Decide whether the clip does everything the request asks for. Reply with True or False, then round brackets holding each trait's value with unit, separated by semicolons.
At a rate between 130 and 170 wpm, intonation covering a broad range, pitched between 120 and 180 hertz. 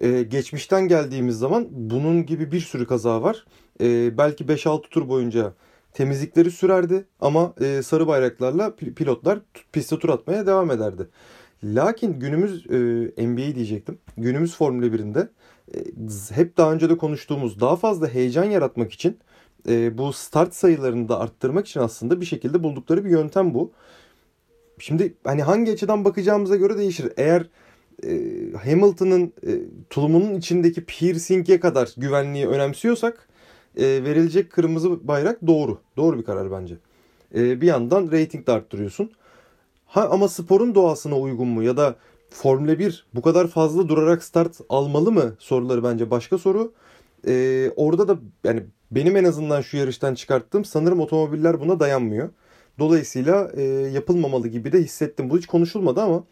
True (140 wpm; 5.9 semitones; 160 Hz)